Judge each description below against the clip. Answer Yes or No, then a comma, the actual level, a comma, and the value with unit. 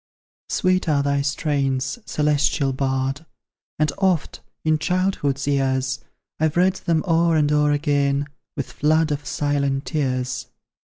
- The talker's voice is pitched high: No, medium, 145 Hz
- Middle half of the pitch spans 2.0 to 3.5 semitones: Yes, narrow, 2.4 semitones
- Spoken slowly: Yes, slow, 125 wpm